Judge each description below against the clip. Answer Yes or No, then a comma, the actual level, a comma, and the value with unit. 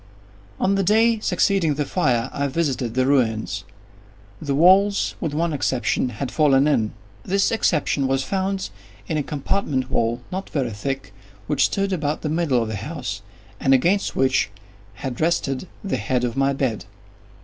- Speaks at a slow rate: No, average, 160 wpm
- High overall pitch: No, medium, 140 Hz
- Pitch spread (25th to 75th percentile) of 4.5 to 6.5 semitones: Yes, wide, 5.4 semitones